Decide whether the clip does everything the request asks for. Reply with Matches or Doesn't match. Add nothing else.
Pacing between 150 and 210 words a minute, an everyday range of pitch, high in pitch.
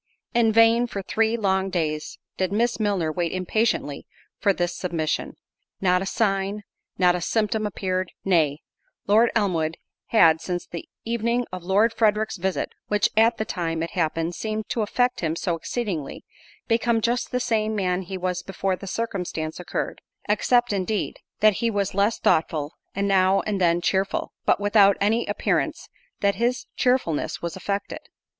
Matches